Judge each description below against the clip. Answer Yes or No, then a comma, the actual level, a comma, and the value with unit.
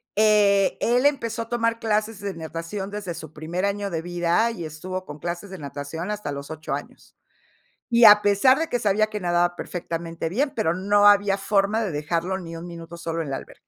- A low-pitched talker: No, high, 190 Hz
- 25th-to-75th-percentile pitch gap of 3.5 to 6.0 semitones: Yes, average, 4.1 semitones